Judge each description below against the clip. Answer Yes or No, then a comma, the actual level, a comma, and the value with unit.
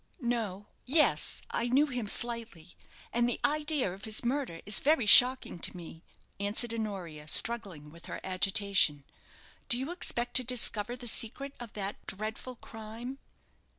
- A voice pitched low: No, high, 225 Hz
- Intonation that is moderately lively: Yes, average, 4.3 semitones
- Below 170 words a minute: Yes, average, 150 wpm